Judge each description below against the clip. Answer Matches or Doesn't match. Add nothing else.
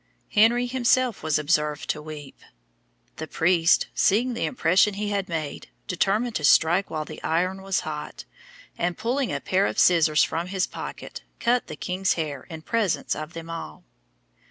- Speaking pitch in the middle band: Matches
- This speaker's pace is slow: Doesn't match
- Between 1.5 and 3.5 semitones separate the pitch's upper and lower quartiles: Doesn't match